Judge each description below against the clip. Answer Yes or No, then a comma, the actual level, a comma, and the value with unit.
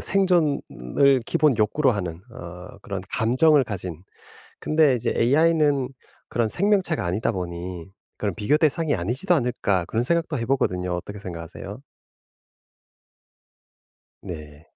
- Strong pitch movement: Yes, wide, 8.7 semitones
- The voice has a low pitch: Yes, low, 115 Hz